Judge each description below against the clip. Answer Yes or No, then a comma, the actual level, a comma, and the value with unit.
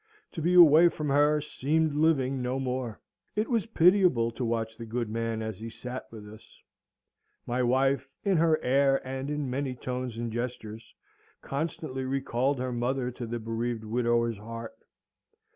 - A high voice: No, low, 130 Hz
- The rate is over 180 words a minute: No, average, 160 wpm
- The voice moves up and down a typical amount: Yes, average, 3.6 semitones